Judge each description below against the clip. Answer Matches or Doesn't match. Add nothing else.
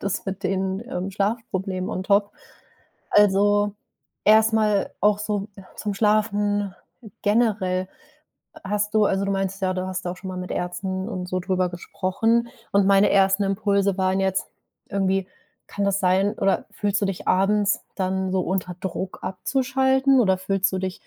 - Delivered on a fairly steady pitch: Matches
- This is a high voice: Matches